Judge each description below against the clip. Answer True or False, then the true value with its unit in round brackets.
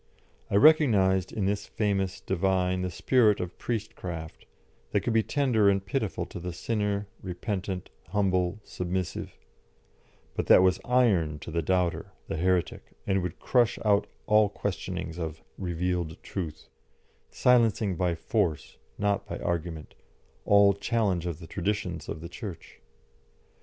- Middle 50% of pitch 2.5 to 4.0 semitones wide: True (3.0 semitones)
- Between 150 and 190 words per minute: False (140 wpm)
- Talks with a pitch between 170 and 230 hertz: False (95 Hz)